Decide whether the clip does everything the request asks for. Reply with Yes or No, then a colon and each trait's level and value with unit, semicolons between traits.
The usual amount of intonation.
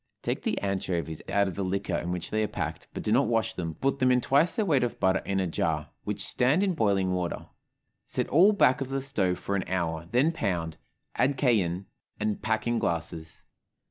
No: wide, 6.4 semitones